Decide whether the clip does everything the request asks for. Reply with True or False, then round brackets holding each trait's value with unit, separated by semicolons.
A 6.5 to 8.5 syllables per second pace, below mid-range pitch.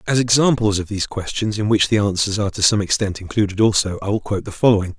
True (6.9 syllables/s; 105 Hz)